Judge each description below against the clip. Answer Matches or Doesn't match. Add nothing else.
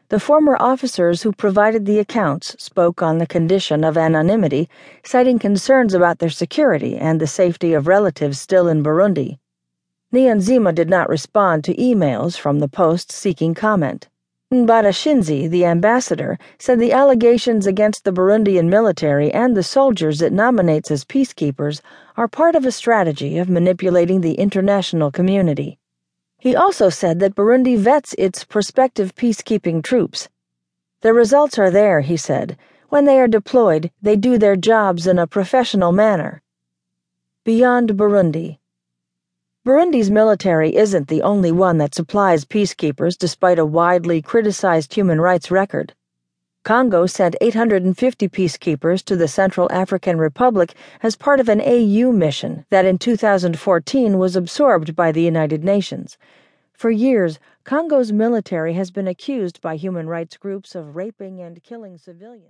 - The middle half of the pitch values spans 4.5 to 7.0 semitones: Matches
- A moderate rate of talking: Matches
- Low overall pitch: Doesn't match